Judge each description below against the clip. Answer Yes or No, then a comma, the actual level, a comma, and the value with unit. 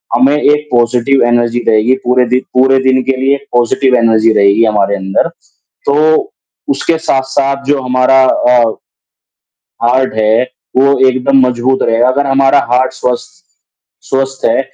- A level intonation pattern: Yes, narrow, 2.3 semitones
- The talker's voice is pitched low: Yes, low, 130 Hz